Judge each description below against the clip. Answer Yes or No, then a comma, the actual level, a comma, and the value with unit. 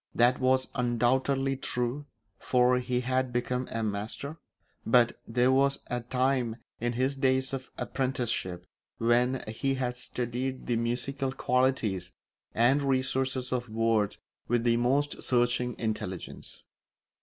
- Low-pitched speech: Yes, low, 125 Hz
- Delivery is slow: Yes, slow, 125 wpm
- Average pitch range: No, narrow, 1.8 semitones